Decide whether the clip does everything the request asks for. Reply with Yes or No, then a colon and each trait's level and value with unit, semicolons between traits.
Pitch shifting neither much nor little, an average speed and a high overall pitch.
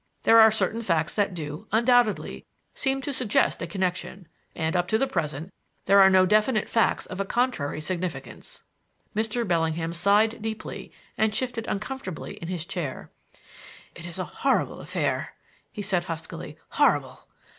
Yes: average, 4.7 semitones; average, 155 wpm; high, 195 Hz